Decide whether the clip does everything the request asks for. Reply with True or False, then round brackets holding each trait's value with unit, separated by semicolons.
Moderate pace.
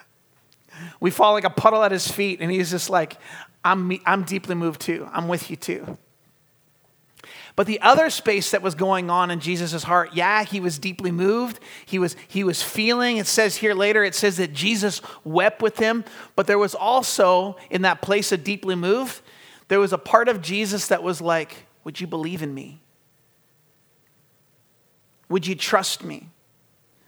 True (180 wpm)